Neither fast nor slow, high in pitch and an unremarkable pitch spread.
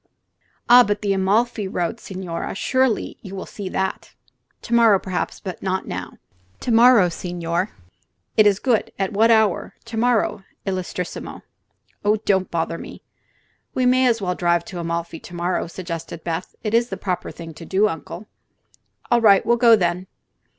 Yes: average, 165 wpm; high, 195 Hz; average, 4.2 semitones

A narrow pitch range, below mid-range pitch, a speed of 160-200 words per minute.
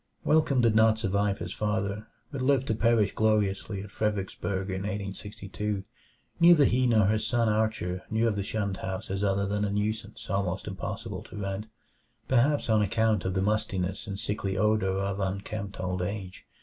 Yes: narrow, 2.1 semitones; low, 105 Hz; average, 175 wpm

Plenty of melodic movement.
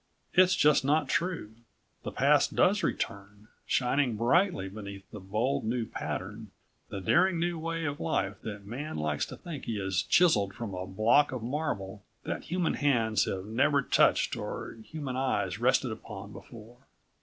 Yes: wide, 6.5 semitones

